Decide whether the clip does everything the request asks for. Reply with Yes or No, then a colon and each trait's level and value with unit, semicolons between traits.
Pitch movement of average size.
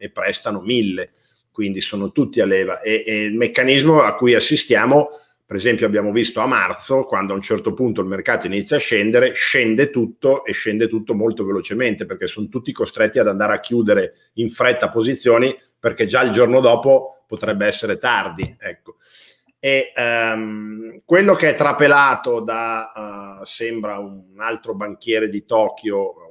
Yes: average, 4.2 semitones